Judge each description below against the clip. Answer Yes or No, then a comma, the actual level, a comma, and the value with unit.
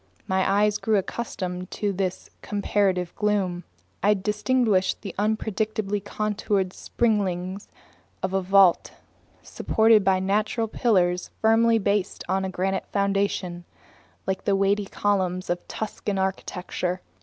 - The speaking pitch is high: Yes, high, 195 Hz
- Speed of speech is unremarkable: No, slow, 120 wpm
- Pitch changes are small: Yes, narrow, 2.1 semitones